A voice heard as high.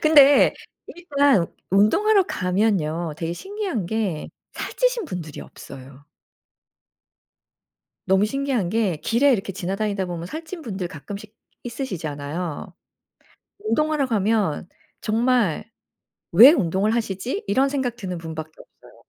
Yes: high, 210 Hz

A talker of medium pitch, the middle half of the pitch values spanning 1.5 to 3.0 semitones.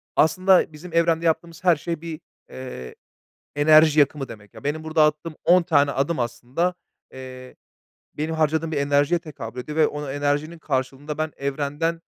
Yes: medium, 150 Hz; average, 2.7 semitones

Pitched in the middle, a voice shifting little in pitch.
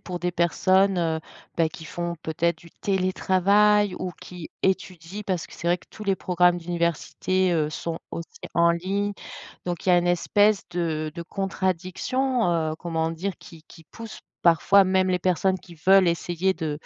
Yes: medium, 175 Hz; narrow, 2.2 semitones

